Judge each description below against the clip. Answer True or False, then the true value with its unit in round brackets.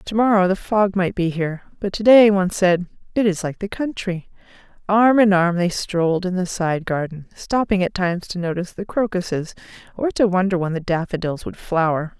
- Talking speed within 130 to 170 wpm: False (190 wpm)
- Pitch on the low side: False (185 Hz)